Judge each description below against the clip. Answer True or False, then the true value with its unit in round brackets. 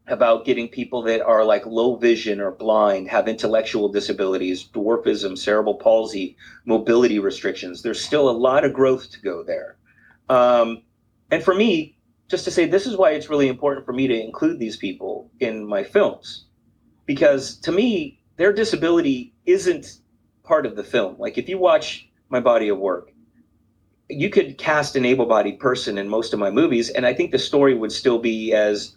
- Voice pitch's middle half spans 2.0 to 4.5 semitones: False (5.5 semitones)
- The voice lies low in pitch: True (125 Hz)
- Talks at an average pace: True (180 wpm)